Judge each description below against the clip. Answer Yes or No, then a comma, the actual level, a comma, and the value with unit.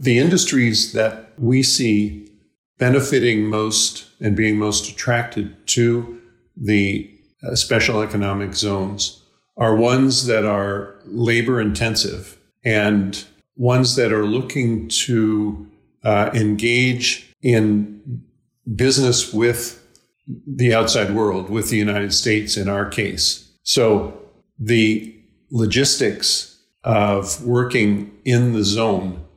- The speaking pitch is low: Yes, low, 110 Hz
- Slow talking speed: Yes, slow, 105 wpm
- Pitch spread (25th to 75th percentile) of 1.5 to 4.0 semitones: Yes, narrow, 2.6 semitones